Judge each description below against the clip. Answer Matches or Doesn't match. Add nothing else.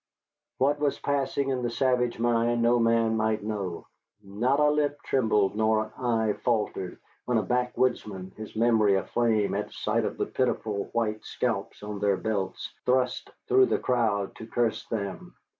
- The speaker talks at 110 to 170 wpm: Matches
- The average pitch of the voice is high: Doesn't match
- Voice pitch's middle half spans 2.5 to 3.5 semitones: Matches